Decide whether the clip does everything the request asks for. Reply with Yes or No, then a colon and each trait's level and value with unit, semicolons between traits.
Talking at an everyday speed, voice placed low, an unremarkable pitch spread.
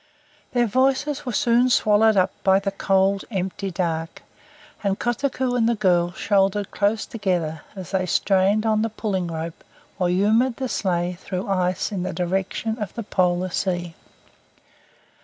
No: average, 160 wpm; high, 195 Hz; average, 3.4 semitones